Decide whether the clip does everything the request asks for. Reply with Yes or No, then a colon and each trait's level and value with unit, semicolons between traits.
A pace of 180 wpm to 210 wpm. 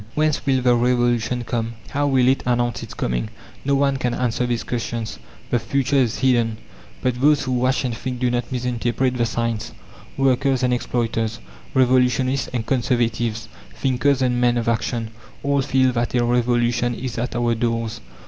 No: average, 170 wpm